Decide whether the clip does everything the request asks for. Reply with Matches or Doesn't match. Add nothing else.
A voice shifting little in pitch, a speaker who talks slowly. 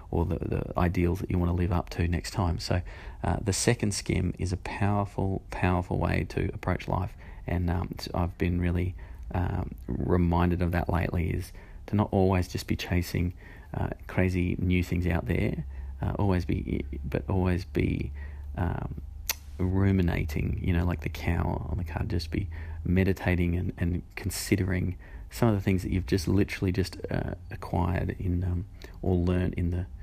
Doesn't match